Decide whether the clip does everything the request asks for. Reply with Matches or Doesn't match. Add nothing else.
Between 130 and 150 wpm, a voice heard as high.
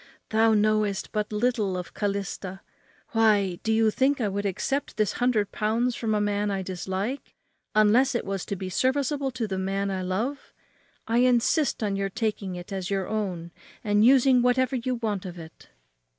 Doesn't match